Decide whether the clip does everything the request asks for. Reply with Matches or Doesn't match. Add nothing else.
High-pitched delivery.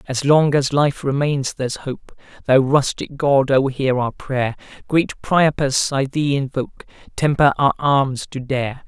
Doesn't match